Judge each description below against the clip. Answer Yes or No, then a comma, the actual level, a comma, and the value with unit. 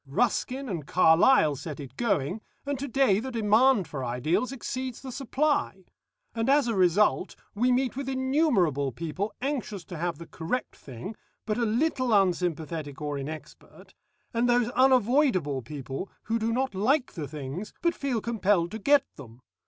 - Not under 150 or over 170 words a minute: Yes, average, 160 wpm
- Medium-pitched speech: No, high, 210 Hz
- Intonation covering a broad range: Yes, wide, 8.1 semitones